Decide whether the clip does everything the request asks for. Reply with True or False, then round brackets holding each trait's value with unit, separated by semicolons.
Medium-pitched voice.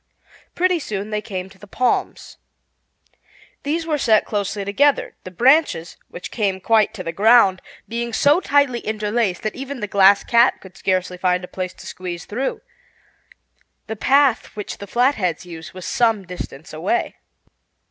False (210 Hz)